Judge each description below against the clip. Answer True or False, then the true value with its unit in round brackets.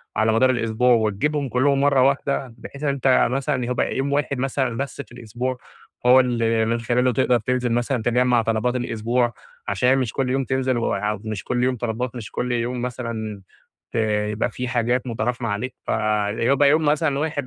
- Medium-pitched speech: False (125 Hz)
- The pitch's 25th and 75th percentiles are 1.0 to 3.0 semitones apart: True (2.4 semitones)